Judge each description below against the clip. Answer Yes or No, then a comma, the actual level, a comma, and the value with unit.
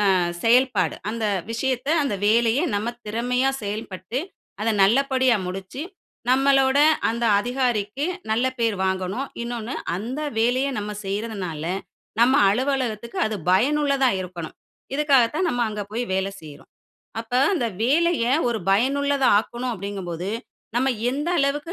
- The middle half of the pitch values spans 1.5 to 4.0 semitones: No, average, 4.4 semitones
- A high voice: Yes, high, 235 Hz